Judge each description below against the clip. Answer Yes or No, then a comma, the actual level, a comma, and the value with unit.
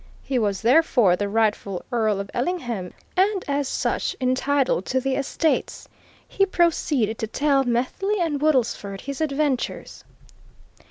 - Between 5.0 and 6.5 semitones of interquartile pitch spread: Yes, wide, 5.4 semitones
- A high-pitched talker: Yes, very high, 260 Hz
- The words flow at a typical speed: No, slow, 130 wpm